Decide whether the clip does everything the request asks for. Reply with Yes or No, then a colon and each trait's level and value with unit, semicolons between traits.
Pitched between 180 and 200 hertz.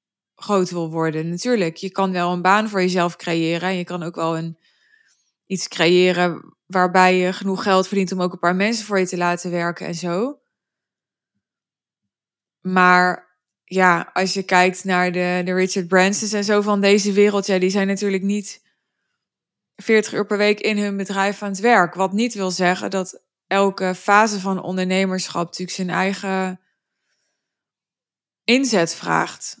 Yes: high, 190 Hz